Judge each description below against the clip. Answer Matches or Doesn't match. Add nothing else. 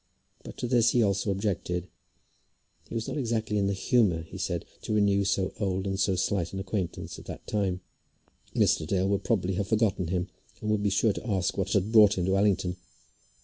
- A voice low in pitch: Matches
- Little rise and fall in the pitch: Matches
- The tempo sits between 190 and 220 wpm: Matches